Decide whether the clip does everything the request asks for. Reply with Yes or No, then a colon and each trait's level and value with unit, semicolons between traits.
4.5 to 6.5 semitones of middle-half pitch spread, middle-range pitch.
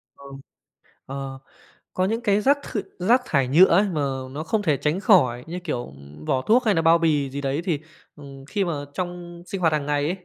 Yes: average, 5.2 semitones; medium, 160 Hz